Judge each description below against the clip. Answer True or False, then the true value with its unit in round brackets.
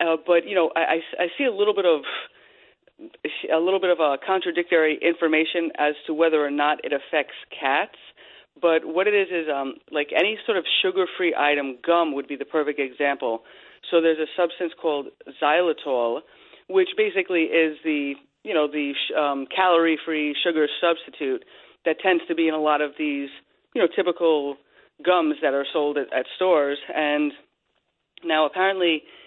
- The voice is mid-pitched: True (165 Hz)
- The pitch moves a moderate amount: True (3.5 semitones)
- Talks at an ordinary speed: True (170 wpm)